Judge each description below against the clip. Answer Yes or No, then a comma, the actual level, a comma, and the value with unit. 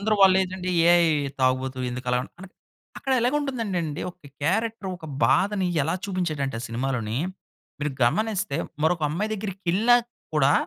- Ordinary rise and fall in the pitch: No, wide, 6.7 semitones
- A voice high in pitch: No, medium, 180 Hz